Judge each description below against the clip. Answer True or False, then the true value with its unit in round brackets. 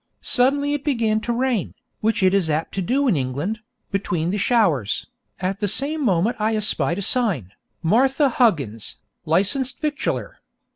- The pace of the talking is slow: False (160 wpm)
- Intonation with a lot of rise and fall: True (6.9 semitones)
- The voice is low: False (210 Hz)